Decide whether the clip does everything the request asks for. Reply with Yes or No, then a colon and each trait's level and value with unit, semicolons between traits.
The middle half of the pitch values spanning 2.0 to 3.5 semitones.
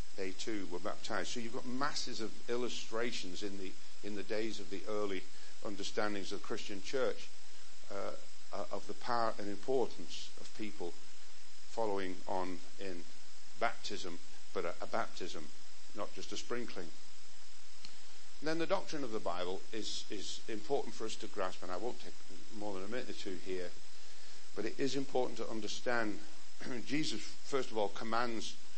No: average, 4.4 semitones